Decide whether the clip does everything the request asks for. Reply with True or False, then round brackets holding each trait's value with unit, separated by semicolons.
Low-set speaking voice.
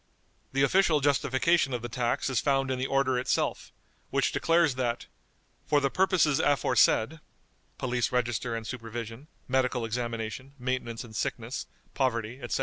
True (130 Hz)